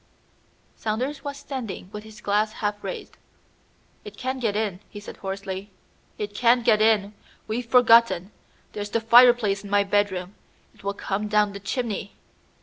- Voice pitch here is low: No, high, 210 Hz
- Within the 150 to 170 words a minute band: Yes, average, 155 wpm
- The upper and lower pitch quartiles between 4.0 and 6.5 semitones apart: No, narrow, 2.5 semitones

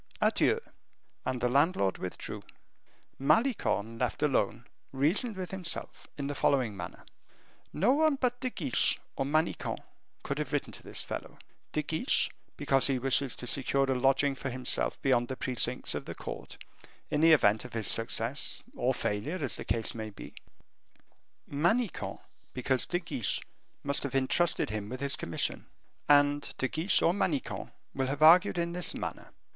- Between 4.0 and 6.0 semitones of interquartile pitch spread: Yes, average, 5.1 semitones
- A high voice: No, medium, 140 Hz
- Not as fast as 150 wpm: No, average, 160 wpm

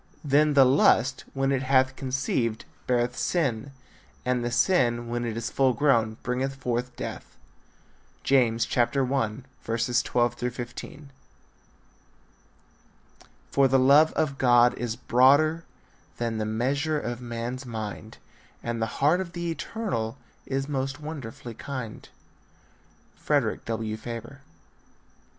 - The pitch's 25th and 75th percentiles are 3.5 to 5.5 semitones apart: No, average, 2.7 semitones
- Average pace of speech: No, slow, 115 wpm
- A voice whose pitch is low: Yes, low, 125 Hz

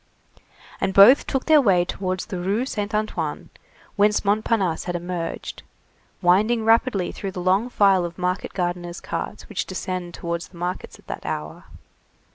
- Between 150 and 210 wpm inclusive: Yes, average, 155 wpm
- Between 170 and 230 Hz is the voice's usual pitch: Yes, high, 190 Hz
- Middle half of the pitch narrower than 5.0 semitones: Yes, average, 3.2 semitones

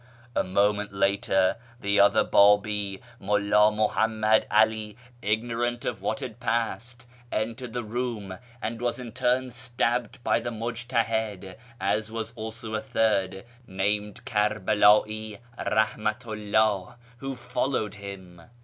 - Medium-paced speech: No, slow, 120 wpm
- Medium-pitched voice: No, low, 110 Hz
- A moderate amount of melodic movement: No, narrow, 2.3 semitones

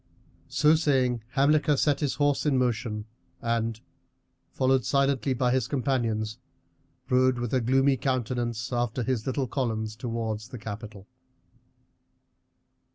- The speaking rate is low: Yes, slow, 120 wpm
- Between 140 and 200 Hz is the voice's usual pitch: No, low, 125 Hz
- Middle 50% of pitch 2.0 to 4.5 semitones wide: Yes, average, 2.8 semitones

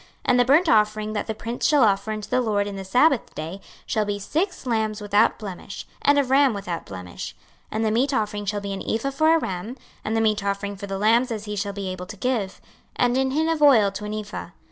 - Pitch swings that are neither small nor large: Yes, average, 3.8 semitones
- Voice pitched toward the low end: No, high, 215 Hz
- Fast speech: Yes, fast, 255 wpm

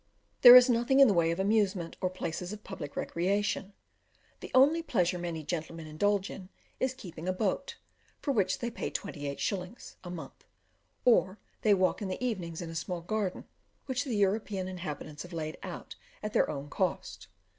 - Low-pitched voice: No, medium, 185 Hz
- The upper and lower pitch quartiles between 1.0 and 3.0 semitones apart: No, average, 4.2 semitones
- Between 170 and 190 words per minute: Yes, average, 175 wpm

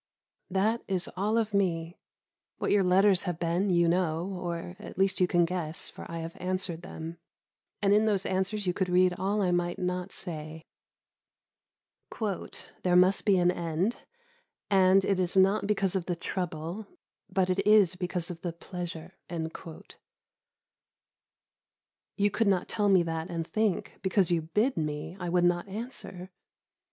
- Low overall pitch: No, medium, 180 Hz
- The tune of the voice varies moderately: No, narrow, 2.3 semitones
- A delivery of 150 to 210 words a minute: Yes, average, 160 wpm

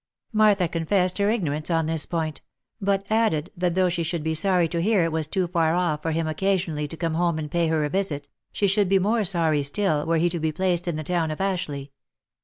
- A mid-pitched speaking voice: Yes, medium, 170 Hz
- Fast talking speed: Yes, fast, 240 wpm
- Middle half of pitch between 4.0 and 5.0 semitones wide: No, average, 3.2 semitones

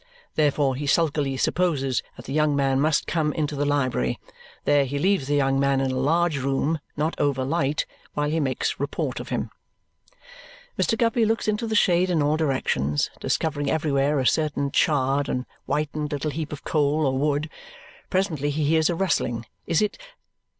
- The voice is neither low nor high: Yes, medium, 145 Hz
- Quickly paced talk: No, average, 180 wpm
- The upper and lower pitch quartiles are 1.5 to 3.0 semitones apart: Yes, narrow, 2.6 semitones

